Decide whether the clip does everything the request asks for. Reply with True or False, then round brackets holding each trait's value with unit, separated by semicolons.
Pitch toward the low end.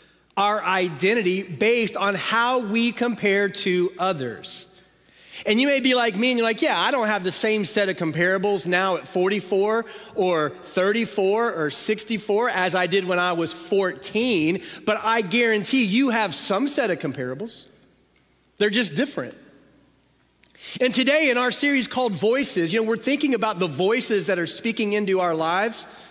False (210 Hz)